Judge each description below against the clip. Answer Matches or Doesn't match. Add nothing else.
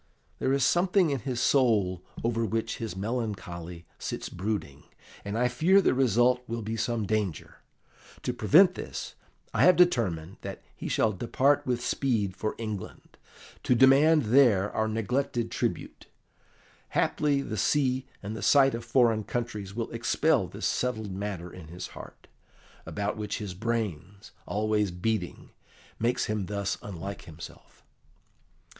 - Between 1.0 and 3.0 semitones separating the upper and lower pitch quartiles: Doesn't match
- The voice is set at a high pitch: Doesn't match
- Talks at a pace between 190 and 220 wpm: Doesn't match